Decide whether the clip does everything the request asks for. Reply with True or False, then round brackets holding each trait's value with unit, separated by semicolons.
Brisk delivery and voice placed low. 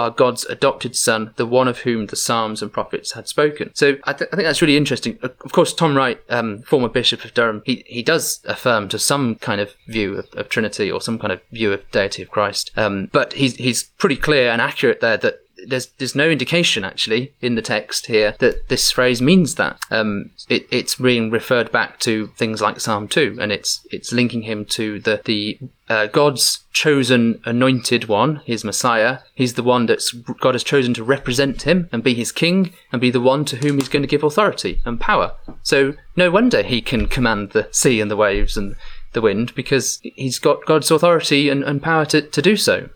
True (215 wpm; 125 Hz)